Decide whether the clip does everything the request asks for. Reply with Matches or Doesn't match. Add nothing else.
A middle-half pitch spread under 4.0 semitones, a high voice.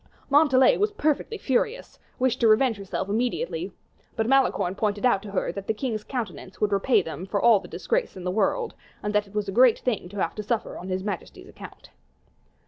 Doesn't match